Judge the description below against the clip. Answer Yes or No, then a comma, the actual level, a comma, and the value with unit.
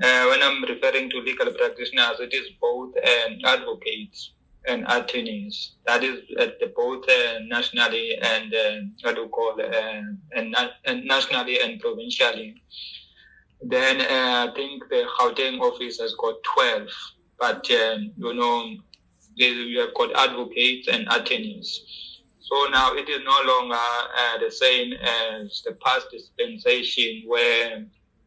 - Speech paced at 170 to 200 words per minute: No, slow, 135 wpm